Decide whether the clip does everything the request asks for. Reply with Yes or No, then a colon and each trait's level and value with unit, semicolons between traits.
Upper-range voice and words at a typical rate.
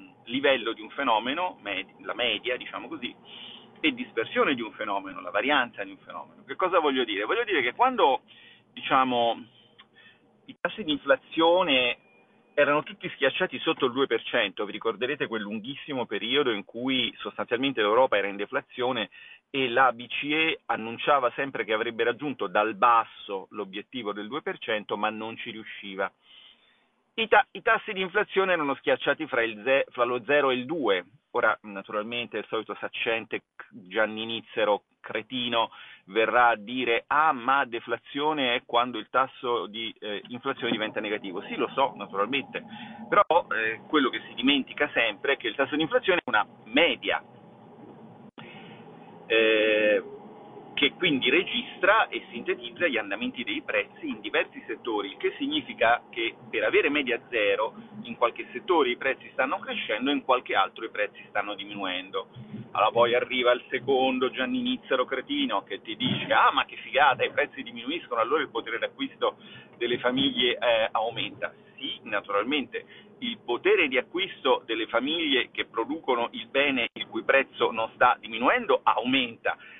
No: medium, 140 Hz; average, 155 wpm